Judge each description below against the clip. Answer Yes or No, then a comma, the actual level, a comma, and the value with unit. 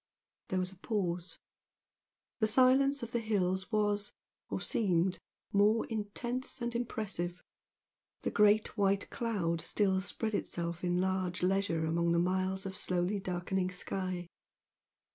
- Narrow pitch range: No, average, 3.2 semitones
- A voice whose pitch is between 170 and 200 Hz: Yes, high, 190 Hz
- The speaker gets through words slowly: Yes, slow, 130 wpm